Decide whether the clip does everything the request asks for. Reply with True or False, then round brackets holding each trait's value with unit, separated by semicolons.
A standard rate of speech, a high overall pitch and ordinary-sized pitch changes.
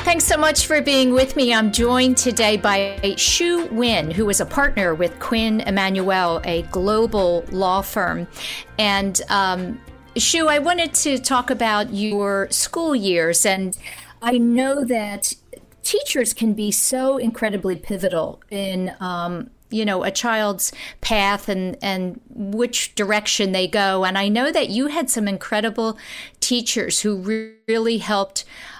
True (150 wpm; 215 Hz; 4.3 semitones)